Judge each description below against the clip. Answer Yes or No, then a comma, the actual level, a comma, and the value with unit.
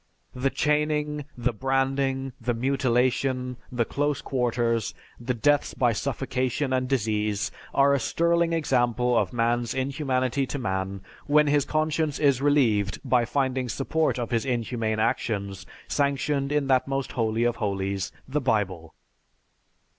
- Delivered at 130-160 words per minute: Yes, slow, 135 wpm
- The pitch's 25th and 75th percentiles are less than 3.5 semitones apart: Yes, average, 3.1 semitones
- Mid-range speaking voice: No, low, 130 Hz